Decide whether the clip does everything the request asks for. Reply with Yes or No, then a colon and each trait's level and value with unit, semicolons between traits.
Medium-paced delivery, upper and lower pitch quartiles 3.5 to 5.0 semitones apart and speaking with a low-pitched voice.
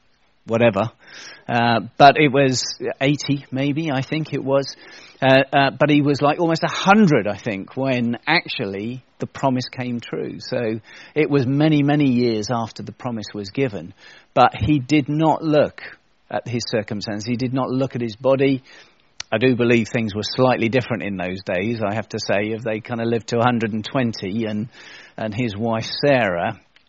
Yes: average, 175 wpm; average, 3.8 semitones; low, 125 Hz